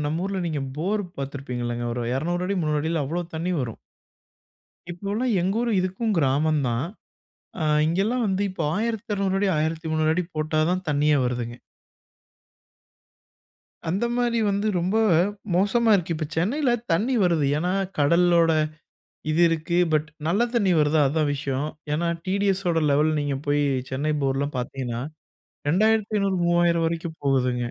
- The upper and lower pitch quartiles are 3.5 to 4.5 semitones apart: No, average, 5.0 semitones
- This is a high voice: No, medium, 165 Hz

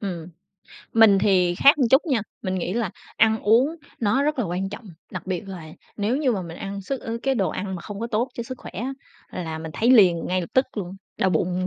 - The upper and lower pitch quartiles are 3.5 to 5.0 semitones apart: Yes, average, 4.6 semitones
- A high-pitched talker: Yes, high, 205 Hz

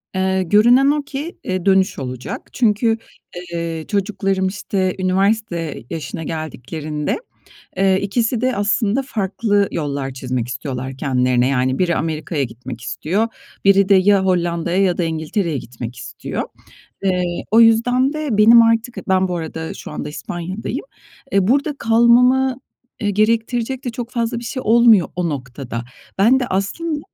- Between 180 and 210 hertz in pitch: Yes, high, 190 Hz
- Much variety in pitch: Yes, wide, 6.3 semitones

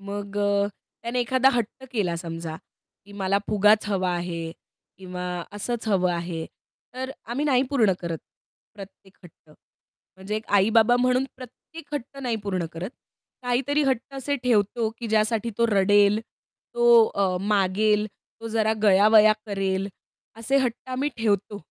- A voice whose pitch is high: Yes, high, 210 Hz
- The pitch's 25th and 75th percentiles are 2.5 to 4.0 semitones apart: Yes, average, 3.6 semitones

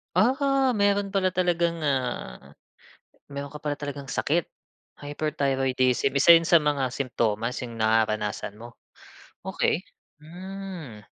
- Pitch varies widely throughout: Yes, wide, 5.9 semitones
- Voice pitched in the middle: Yes, medium, 145 Hz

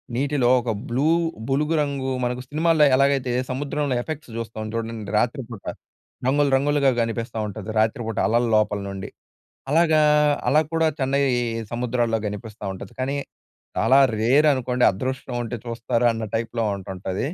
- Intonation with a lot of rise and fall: No, average, 3.6 semitones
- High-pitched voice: No, low, 125 Hz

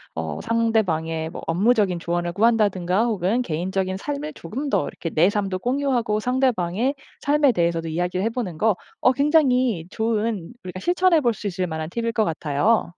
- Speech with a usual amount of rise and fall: No, wide, 5.9 semitones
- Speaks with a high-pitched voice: Yes, high, 210 Hz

